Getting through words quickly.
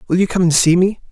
Yes: fast, 325 wpm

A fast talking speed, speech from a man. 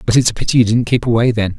Yes: fast, 340 wpm; male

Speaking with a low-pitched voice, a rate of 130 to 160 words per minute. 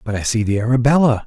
No: low, 120 Hz; fast, 240 wpm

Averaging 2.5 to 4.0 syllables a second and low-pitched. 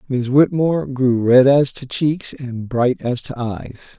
Yes: 3.9 syllables/s; low, 130 Hz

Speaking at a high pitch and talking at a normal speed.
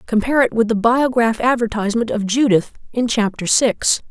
Yes: high, 230 Hz; average, 160 wpm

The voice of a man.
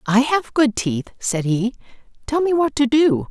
No: female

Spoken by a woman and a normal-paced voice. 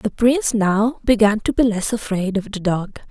No: female; fast, 215 wpm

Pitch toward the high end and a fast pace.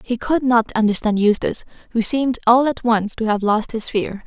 Yes: high, 230 Hz; fast, 210 wpm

